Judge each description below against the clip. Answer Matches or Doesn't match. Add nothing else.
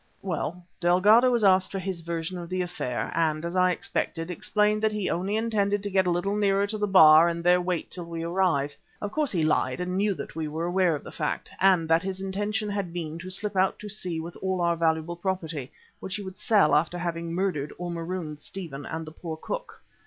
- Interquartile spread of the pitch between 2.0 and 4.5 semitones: Matches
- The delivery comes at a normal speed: Doesn't match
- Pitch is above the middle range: Doesn't match